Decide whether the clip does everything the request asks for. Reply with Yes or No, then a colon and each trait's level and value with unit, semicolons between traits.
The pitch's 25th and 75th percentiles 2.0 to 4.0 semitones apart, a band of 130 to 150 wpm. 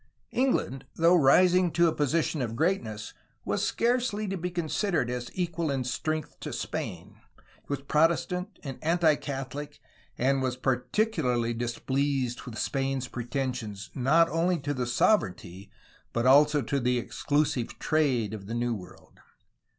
No: average, 5.3 semitones; average, 140 wpm